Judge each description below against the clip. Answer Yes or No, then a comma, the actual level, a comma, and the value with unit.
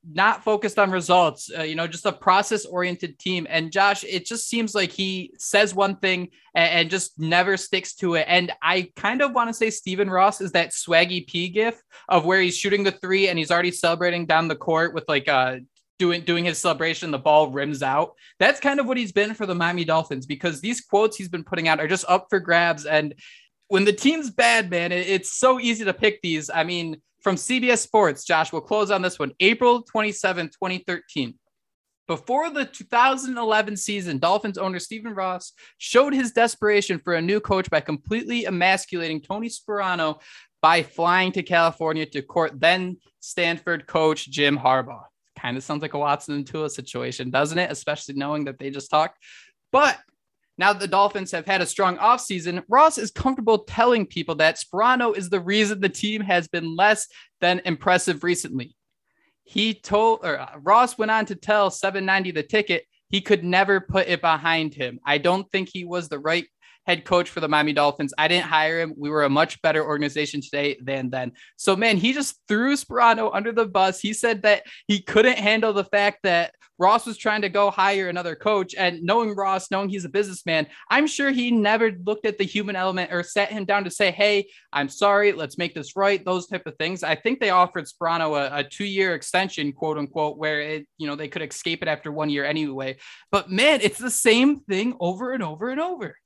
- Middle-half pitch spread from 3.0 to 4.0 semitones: No, average, 4.6 semitones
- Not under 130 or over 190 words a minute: No, fast, 205 wpm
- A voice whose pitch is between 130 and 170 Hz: No, medium, 185 Hz